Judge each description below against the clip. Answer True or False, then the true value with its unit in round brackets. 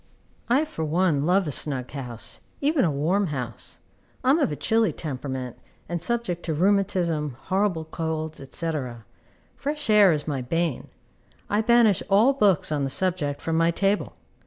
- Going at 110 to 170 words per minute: True (160 wpm)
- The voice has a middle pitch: True (170 Hz)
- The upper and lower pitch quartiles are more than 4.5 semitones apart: True (5.6 semitones)